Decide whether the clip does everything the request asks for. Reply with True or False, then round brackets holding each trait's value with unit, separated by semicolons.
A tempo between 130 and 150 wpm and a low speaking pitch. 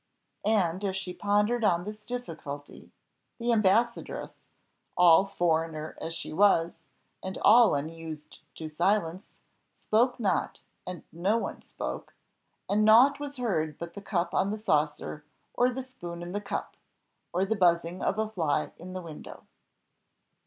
False (145 wpm; 185 Hz)